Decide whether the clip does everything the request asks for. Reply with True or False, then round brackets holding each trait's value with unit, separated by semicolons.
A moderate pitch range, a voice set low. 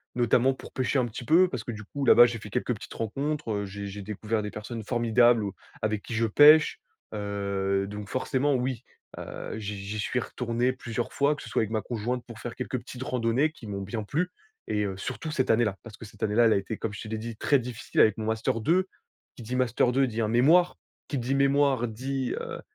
True (3.2 semitones; 115 Hz)